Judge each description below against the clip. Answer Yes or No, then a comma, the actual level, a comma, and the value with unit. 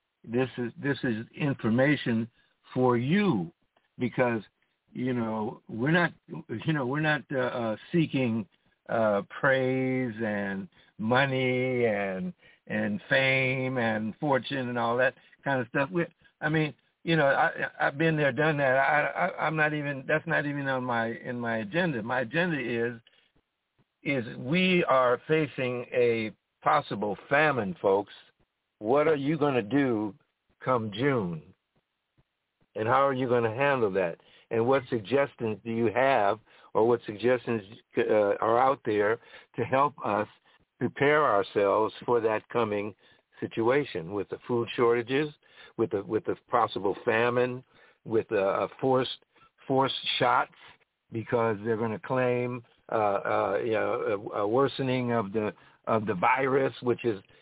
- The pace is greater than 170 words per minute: No, average, 145 wpm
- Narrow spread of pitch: No, average, 3.5 semitones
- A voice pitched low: Yes, low, 125 Hz